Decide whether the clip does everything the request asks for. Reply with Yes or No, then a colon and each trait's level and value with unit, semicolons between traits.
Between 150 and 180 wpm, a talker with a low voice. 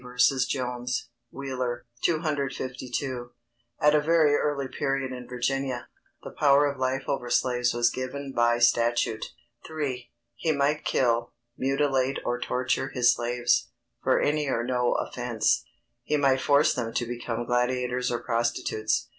No: average, 140 wpm; low, 130 Hz